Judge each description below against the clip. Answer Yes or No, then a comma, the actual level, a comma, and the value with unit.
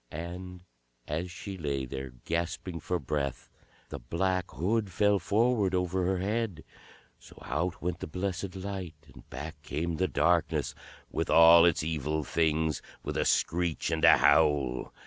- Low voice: Yes, very low, 85 Hz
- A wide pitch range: No, average, 3.3 semitones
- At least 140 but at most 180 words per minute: Yes, average, 150 wpm